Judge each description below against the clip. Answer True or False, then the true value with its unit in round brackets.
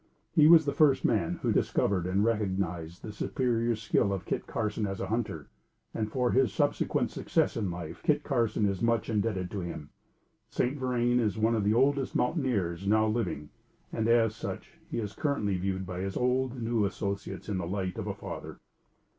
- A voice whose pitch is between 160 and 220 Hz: False (110 Hz)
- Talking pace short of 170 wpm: False (190 wpm)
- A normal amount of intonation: True (3.9 semitones)